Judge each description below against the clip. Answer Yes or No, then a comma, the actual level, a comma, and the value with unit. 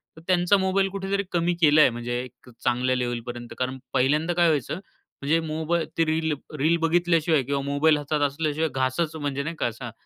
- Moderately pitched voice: Yes, medium, 155 Hz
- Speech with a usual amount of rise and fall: Yes, average, 4.2 semitones